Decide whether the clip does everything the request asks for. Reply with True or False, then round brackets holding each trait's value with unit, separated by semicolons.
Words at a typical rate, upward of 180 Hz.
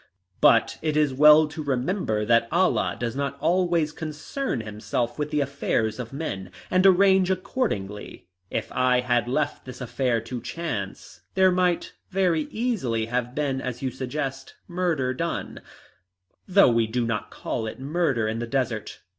False (155 wpm; 135 Hz)